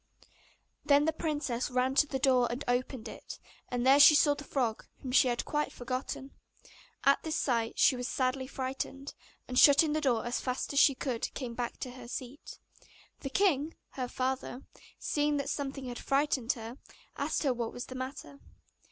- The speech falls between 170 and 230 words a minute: Yes, average, 185 wpm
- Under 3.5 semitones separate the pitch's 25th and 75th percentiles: Yes, narrow, 2.4 semitones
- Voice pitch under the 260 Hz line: No, very high, 265 Hz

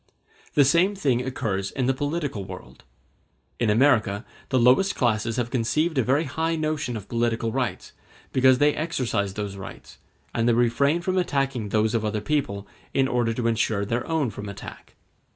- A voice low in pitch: Yes, low, 125 Hz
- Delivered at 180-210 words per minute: No, average, 170 wpm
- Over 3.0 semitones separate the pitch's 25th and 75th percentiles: Yes, average, 4.6 semitones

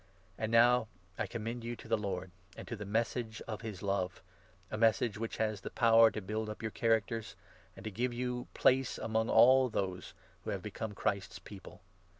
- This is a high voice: No, low, 110 Hz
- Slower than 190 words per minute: No, fast, 205 wpm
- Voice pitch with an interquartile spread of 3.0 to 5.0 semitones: No, narrow, 2.6 semitones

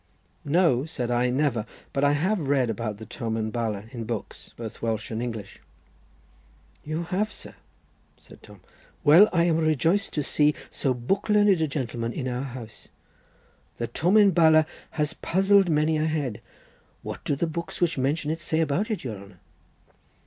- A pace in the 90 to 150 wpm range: No, average, 170 wpm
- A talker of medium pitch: Yes, medium, 145 Hz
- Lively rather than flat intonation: Yes, wide, 5.7 semitones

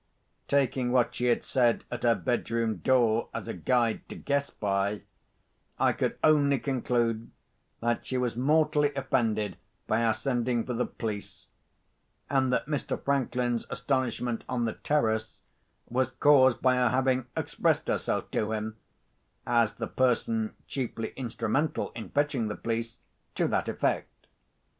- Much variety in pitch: No, narrow, 2.6 semitones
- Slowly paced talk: No, average, 145 wpm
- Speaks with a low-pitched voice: Yes, low, 125 Hz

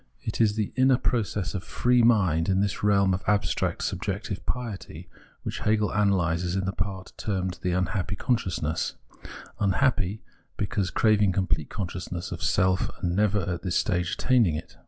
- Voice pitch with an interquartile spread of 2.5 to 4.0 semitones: Yes, average, 2.8 semitones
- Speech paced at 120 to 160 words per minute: No, average, 175 wpm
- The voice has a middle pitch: No, very low, 95 Hz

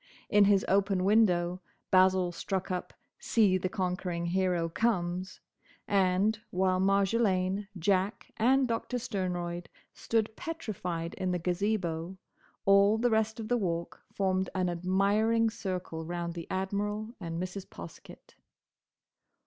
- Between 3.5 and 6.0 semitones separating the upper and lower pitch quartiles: No, average, 2.7 semitones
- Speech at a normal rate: No, slow, 125 wpm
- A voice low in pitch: No, high, 190 Hz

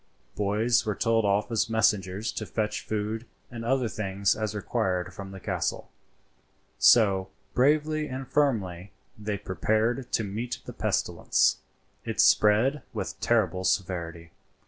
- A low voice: Yes, low, 105 Hz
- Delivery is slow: Yes, slow, 130 wpm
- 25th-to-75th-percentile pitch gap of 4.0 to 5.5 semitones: No, average, 3.5 semitones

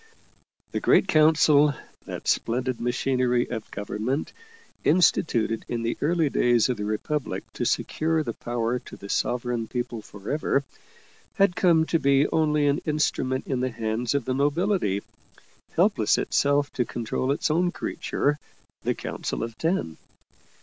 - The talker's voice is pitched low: Yes, low, 130 Hz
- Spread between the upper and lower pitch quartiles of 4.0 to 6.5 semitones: Yes, average, 4.5 semitones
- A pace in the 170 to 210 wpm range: No, average, 145 wpm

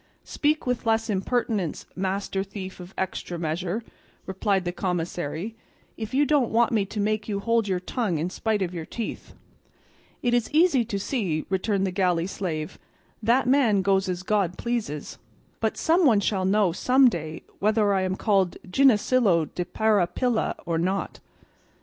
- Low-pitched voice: No, high, 200 Hz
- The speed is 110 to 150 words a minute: No, average, 160 wpm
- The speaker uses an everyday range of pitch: Yes, average, 4.1 semitones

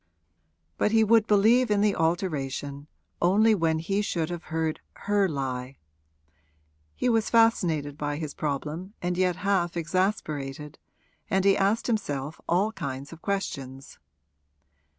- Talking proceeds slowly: Yes, slow, 130 wpm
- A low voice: No, medium, 175 Hz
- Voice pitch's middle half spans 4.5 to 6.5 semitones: Yes, wide, 5.6 semitones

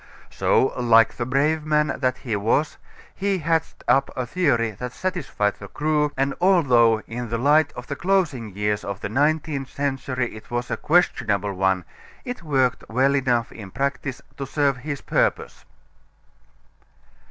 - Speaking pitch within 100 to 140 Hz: Yes, low, 135 Hz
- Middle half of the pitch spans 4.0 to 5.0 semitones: Yes, average, 4.6 semitones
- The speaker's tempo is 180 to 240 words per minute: No, average, 155 wpm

